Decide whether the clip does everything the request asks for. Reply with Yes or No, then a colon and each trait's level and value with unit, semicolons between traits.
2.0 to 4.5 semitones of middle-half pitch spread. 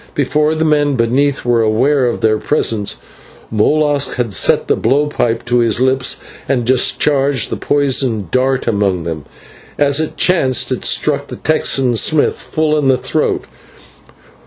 Yes: average, 4.0 semitones